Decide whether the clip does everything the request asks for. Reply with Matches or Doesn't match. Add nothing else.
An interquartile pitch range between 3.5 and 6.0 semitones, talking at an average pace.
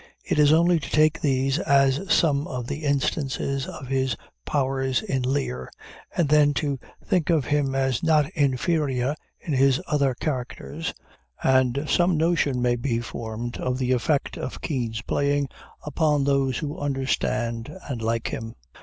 Doesn't match